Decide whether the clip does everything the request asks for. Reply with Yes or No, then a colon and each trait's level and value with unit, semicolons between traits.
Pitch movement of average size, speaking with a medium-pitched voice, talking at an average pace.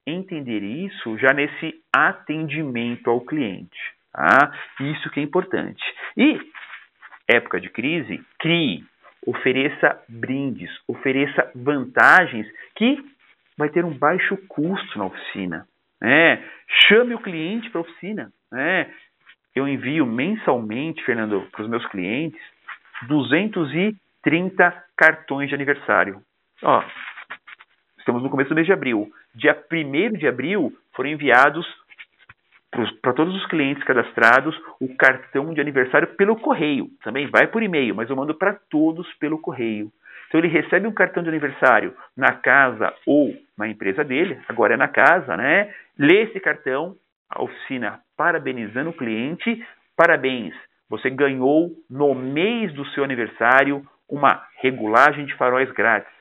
Yes: average, 5.0 semitones; medium, 150 Hz; average, 130 wpm